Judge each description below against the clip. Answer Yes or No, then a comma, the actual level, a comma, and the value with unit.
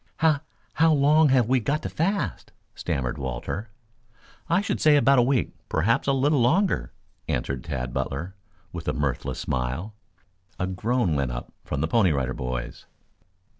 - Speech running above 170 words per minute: No, average, 160 wpm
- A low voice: Yes, low, 105 Hz